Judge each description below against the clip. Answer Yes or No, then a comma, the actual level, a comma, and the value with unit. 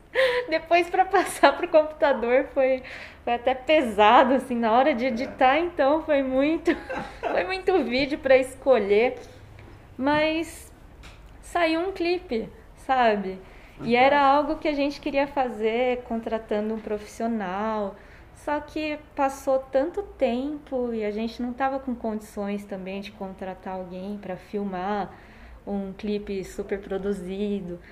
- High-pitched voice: Yes, very high, 255 Hz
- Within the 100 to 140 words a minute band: Yes, average, 130 wpm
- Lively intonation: Yes, wide, 6.0 semitones